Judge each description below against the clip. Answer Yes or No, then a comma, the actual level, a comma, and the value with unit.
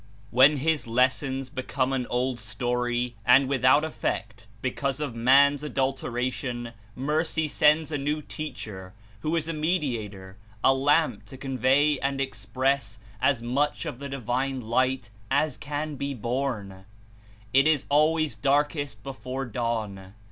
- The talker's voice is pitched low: Yes, low, 130 Hz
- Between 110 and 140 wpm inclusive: Yes, slow, 135 wpm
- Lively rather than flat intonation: No, average, 3.3 semitones